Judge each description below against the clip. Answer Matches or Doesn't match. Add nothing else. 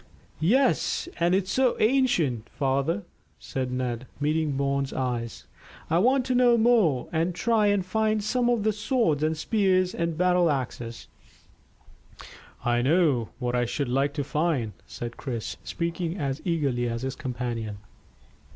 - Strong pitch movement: Matches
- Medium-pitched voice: Matches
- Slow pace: Doesn't match